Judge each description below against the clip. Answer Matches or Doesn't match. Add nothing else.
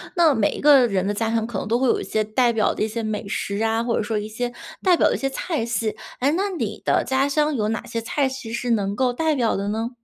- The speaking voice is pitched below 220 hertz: Doesn't match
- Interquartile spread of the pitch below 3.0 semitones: Doesn't match